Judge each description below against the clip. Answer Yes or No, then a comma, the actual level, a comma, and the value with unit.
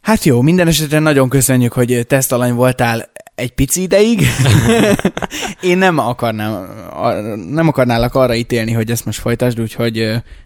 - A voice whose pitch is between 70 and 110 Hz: No, low, 125 Hz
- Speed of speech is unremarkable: Yes, average, 140 wpm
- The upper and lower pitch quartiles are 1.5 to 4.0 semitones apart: No, average, 4.7 semitones